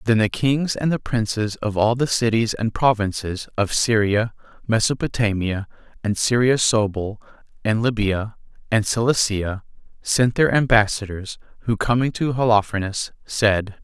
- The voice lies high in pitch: No, low, 110 Hz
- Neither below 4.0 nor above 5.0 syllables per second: Yes, 4.5 syllables/s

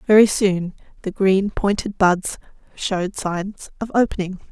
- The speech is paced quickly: No, slow, 135 wpm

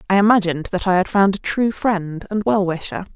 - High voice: Yes, high, 195 Hz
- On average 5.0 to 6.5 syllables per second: Yes, 5.7 syllables/s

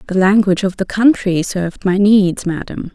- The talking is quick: No, average, 185 wpm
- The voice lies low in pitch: No, high, 195 Hz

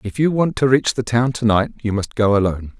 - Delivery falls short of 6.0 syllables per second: Yes, 5.8 syllables/s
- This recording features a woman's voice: No, male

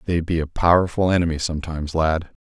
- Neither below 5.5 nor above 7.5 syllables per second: Yes, 6.4 syllables/s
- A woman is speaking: No, male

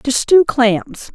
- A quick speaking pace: No, average, 155 wpm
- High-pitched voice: Yes, very high, 255 Hz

